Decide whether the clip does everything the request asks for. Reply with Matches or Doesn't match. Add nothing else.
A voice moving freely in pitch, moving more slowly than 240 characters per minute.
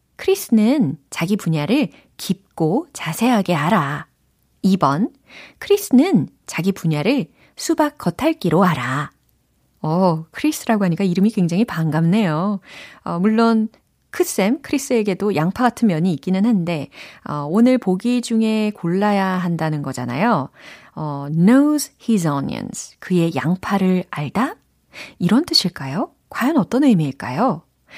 Doesn't match